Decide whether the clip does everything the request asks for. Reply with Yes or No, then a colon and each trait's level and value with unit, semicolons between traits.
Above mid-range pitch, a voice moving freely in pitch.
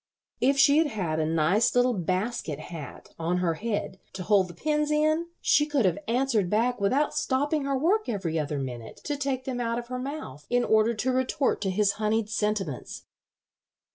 Yes: high, 225 Hz; wide, 6.7 semitones